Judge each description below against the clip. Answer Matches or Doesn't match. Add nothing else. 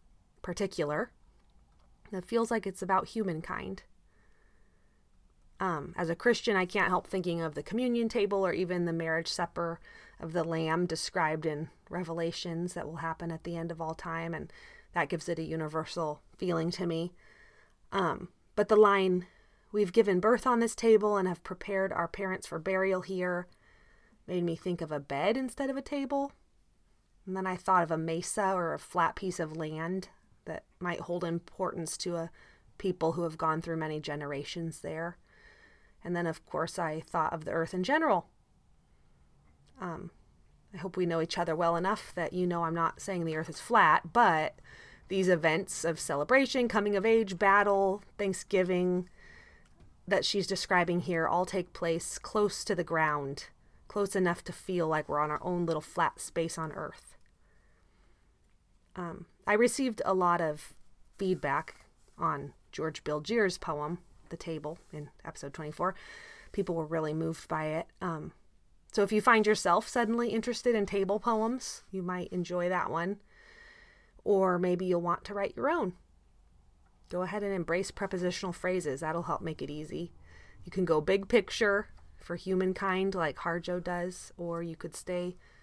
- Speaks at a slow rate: Doesn't match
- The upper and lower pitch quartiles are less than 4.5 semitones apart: Matches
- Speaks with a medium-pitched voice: Matches